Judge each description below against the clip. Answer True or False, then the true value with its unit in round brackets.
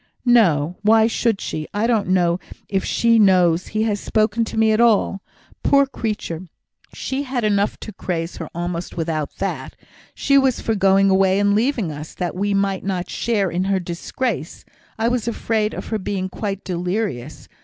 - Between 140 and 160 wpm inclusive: False (175 wpm)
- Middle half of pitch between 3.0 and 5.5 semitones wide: True (3.8 semitones)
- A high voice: True (200 Hz)